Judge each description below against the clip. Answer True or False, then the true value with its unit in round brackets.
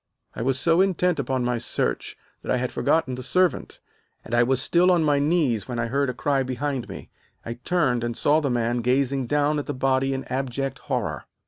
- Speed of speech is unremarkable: False (215 wpm)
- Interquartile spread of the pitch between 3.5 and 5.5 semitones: False (3.1 semitones)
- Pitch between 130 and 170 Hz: True (135 Hz)